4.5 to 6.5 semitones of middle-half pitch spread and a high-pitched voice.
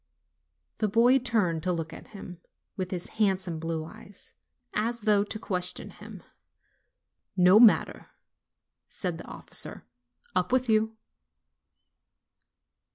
No: average, 3.7 semitones; high, 200 Hz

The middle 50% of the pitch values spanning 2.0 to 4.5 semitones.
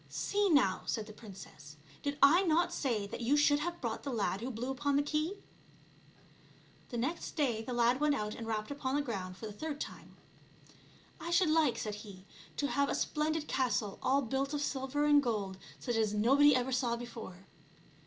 No: average, 5.1 semitones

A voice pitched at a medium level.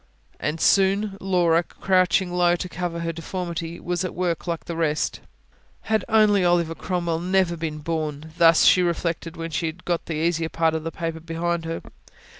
Yes: medium, 170 Hz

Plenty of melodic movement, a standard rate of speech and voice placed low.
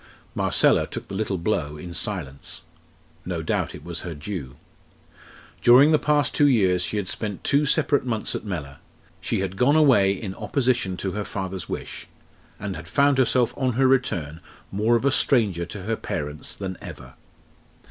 Yes: wide, 6.3 semitones; average, 175 wpm; low, 100 Hz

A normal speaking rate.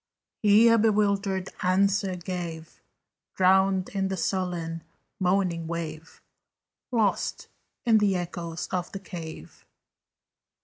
No: slow, 100 wpm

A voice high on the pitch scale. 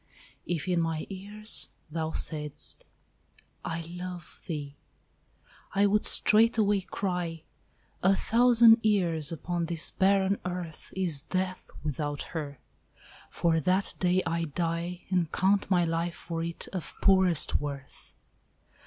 No: medium, 175 Hz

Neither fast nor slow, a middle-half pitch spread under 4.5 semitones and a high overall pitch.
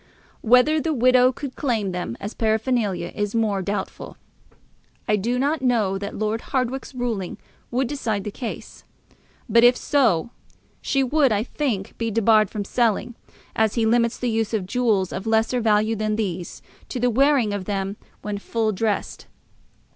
Yes: average, 160 wpm; average, 3.3 semitones; high, 225 Hz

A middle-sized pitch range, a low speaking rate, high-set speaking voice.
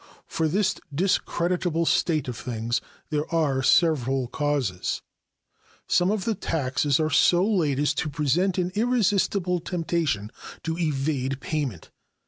No: average, 4.7 semitones; slow, 125 wpm; medium, 155 Hz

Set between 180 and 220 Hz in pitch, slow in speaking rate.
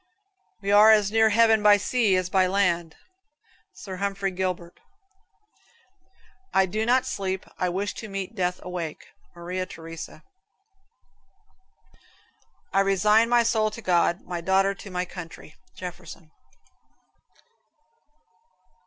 Yes: high, 190 Hz; slow, 120 wpm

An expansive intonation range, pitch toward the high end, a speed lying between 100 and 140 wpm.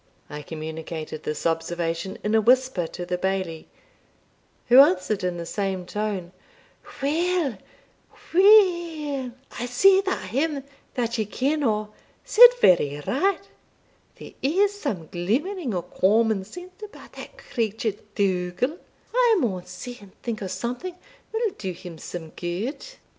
Yes: wide, 8.9 semitones; high, 215 Hz; slow, 135 wpm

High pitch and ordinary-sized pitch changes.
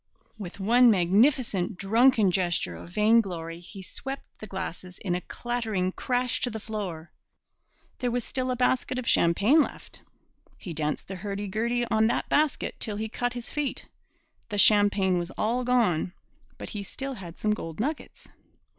Yes: high, 215 Hz; average, 4.8 semitones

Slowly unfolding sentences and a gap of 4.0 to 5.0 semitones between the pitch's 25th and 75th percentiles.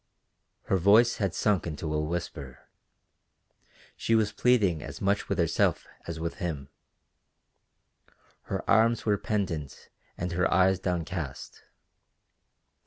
Yes: slow, 115 wpm; average, 4.4 semitones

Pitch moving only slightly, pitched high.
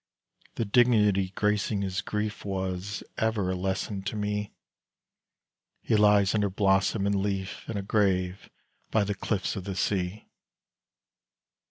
No: narrow, 1.5 semitones; low, 100 Hz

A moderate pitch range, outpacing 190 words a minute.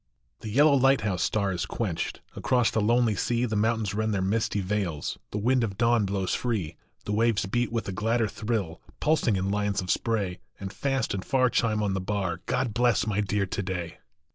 Yes: average, 3.3 semitones; average, 200 wpm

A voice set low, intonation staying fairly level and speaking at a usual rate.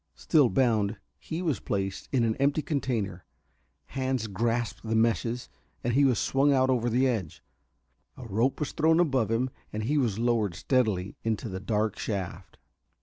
No: low, 115 Hz; average, 3.8 semitones; average, 155 wpm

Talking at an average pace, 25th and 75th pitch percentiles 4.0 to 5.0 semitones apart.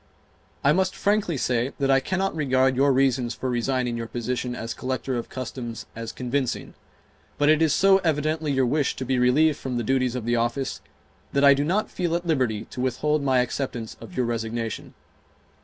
No: average, 190 wpm; average, 3.6 semitones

